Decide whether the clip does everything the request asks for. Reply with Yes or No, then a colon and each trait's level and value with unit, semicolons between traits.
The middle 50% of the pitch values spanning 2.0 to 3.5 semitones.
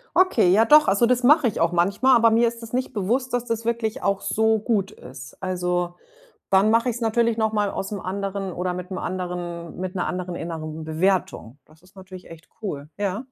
No: average, 4.4 semitones